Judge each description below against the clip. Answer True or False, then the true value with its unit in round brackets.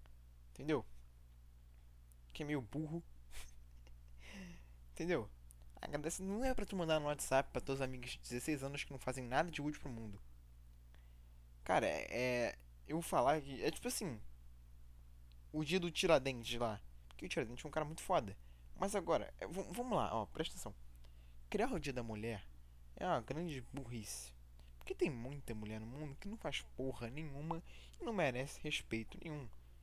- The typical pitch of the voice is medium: False (115 Hz)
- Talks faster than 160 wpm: True (170 wpm)